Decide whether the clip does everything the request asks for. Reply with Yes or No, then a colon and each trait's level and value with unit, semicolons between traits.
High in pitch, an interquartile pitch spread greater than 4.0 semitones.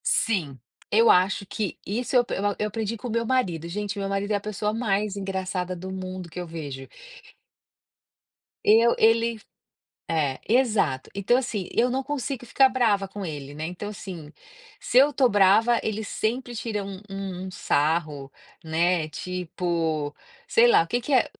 Yes: high, 200 Hz; average, 4.6 semitones